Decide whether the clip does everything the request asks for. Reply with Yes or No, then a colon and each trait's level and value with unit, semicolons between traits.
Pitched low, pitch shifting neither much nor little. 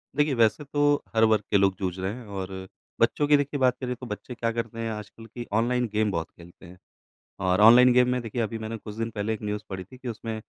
Yes: low, 115 Hz; average, 3.1 semitones